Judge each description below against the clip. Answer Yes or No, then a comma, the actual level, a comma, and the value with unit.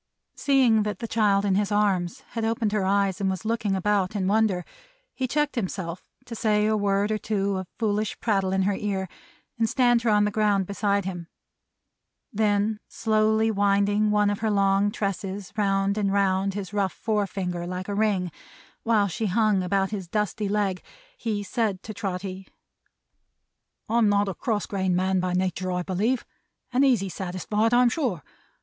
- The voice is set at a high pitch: Yes, high, 205 Hz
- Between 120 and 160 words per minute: No, average, 175 wpm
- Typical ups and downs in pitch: No, narrow, 2.2 semitones